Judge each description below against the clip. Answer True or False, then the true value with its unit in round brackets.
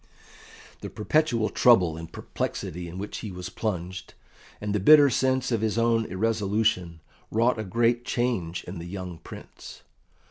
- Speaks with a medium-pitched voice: False (105 Hz)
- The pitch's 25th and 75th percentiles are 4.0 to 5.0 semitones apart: True (4.5 semitones)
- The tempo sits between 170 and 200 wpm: False (150 wpm)